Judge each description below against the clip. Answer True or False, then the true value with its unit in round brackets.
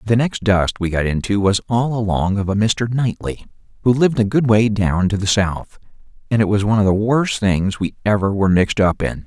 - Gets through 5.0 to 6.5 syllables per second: True (5.5 syllables/s)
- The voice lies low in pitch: True (105 Hz)